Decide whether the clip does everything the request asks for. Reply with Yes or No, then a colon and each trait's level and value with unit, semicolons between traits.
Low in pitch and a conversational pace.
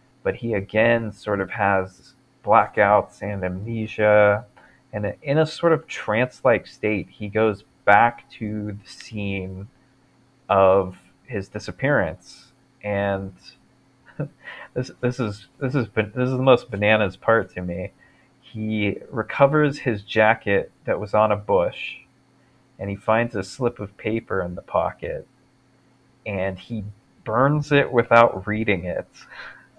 No: low, 110 Hz; slow, 130 wpm